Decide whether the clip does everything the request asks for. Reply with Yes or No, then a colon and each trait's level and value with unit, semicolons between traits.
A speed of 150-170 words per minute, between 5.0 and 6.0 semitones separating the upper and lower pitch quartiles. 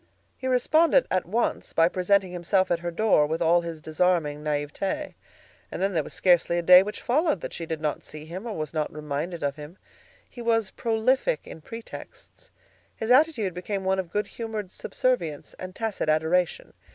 No: average, 185 wpm; wide, 5.6 semitones